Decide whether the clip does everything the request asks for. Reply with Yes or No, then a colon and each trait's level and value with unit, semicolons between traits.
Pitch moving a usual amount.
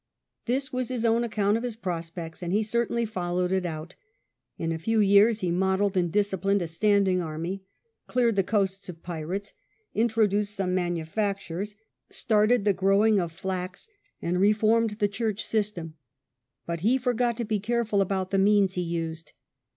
Yes: average, 3.4 semitones